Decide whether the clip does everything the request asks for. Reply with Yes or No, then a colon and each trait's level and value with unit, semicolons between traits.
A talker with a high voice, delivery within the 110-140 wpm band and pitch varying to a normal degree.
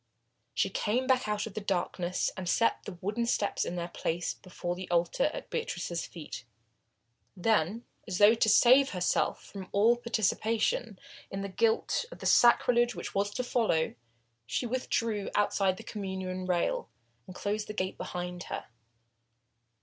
No: high, 205 Hz; average, 155 wpm; average, 4.1 semitones